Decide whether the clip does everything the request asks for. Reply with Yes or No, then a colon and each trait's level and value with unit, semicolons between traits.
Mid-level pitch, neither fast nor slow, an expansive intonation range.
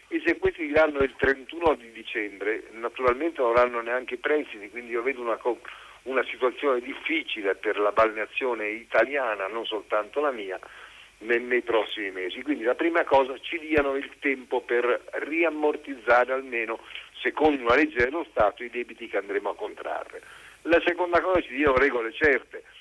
Yes: medium, 145 Hz; average, 160 wpm; wide, 6.2 semitones